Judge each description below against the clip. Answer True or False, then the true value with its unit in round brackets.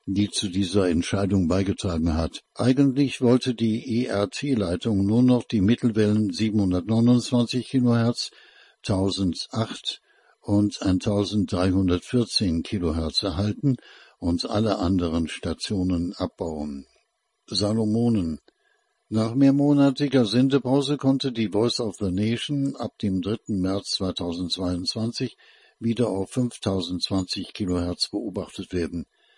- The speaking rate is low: True (95 wpm)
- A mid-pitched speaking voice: False (105 Hz)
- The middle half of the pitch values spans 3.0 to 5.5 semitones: True (4.6 semitones)